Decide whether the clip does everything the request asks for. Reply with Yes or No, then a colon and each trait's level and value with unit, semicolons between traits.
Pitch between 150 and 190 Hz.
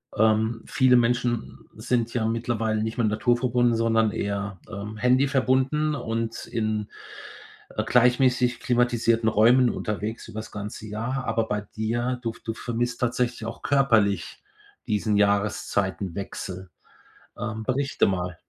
No: low, 115 Hz